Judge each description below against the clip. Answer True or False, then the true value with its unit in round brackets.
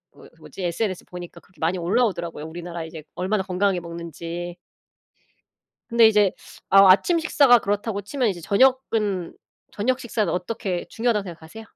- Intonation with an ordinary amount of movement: True (4.4 semitones)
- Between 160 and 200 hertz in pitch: True (190 Hz)